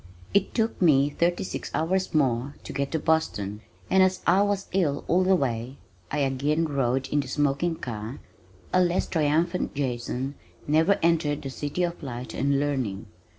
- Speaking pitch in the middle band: Yes, medium, 145 Hz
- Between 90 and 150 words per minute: No, average, 170 wpm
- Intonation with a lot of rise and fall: No, average, 4.5 semitones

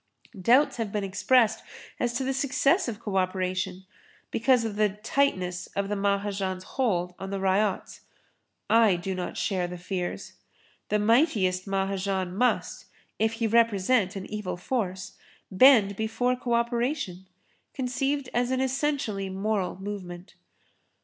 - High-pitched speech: Yes, high, 205 Hz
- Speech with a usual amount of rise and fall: Yes, average, 4.3 semitones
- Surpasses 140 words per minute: No, slow, 135 wpm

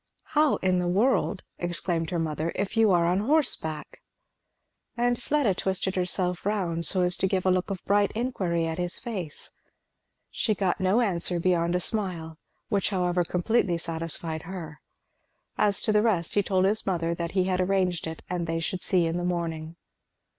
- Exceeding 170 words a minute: Yes, average, 180 wpm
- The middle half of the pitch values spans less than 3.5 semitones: Yes, average, 2.9 semitones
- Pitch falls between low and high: Yes, medium, 180 Hz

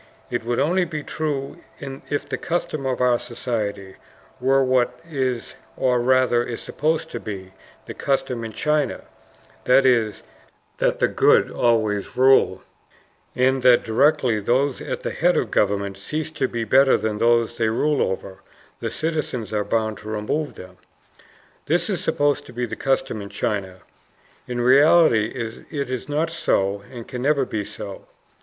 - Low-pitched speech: Yes, low, 125 Hz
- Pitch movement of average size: Yes, average, 4.0 semitones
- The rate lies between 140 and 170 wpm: Yes, average, 160 wpm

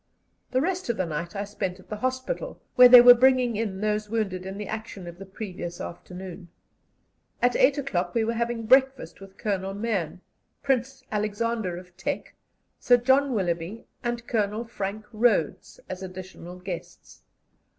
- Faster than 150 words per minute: Yes, average, 160 wpm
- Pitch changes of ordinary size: Yes, average, 4.4 semitones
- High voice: Yes, high, 210 Hz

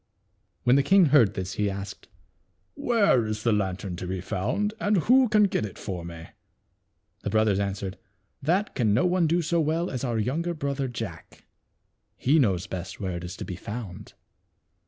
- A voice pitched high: No, low, 115 Hz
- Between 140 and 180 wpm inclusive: No, average, 195 wpm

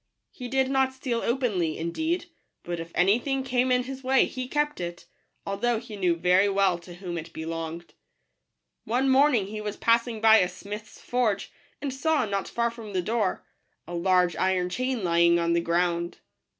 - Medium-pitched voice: No, high, 210 Hz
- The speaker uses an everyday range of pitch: No, wide, 6.3 semitones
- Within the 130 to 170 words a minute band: No, average, 180 wpm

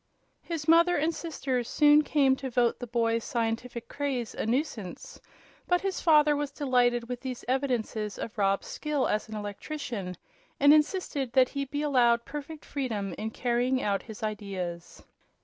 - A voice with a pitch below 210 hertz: No, very high, 250 Hz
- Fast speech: No, average, 160 wpm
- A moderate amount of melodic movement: Yes, average, 4.6 semitones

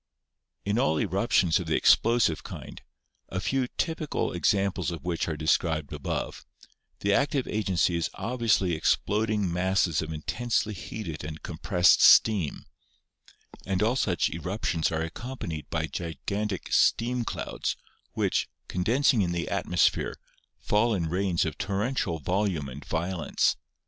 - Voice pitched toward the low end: Yes, very low, 95 Hz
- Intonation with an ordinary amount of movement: Yes, average, 4.8 semitones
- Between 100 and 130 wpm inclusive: No, average, 140 wpm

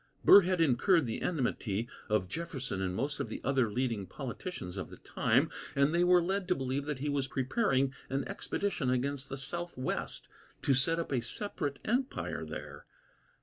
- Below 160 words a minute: No, average, 175 wpm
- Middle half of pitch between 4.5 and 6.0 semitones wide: Yes, average, 5.1 semitones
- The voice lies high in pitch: No, low, 135 Hz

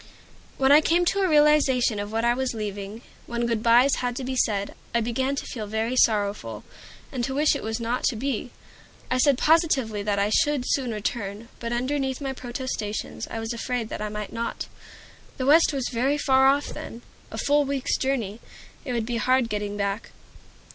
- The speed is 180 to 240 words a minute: Yes, average, 195 wpm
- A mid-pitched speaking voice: No, high, 240 Hz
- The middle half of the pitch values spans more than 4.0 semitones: No, average, 3.6 semitones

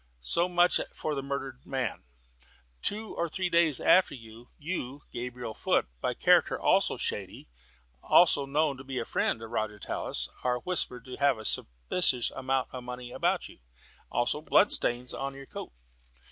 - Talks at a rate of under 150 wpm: No, average, 160 wpm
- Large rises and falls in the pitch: No, average, 3.9 semitones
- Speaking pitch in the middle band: No, low, 130 Hz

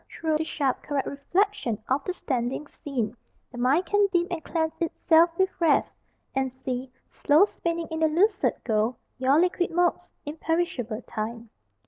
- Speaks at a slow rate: No, average, 155 wpm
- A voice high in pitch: Yes, very high, 305 Hz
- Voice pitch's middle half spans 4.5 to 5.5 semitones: Yes, average, 5.2 semitones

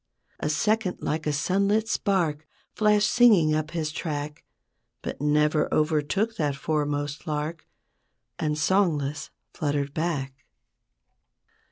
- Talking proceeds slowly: Yes, slow, 110 wpm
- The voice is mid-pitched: Yes, medium, 155 Hz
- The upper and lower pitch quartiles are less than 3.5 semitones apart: No, average, 4.0 semitones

